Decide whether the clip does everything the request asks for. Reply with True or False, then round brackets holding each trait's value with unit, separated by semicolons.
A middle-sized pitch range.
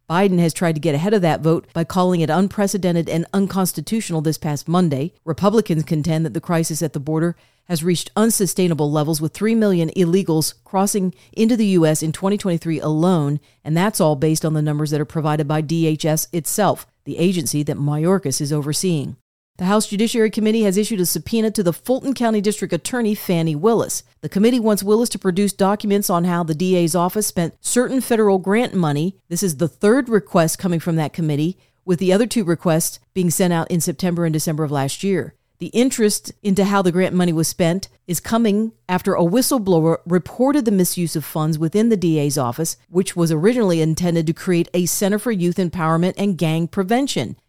True (4.0 semitones)